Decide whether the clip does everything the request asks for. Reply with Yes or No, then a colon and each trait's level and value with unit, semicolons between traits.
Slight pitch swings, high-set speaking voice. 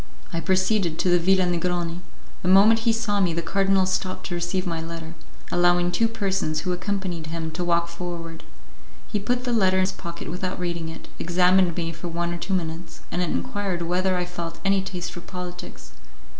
No: narrow, 1.9 semitones; medium, 180 Hz